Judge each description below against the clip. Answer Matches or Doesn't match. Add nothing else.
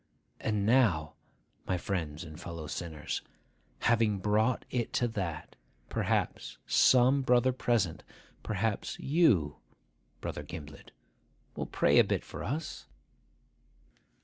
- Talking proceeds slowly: Matches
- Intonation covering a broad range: Matches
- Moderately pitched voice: Doesn't match